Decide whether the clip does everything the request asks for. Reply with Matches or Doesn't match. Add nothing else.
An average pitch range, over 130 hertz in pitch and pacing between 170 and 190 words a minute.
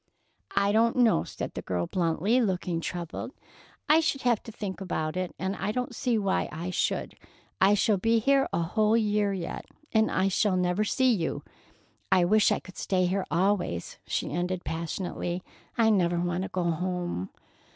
Matches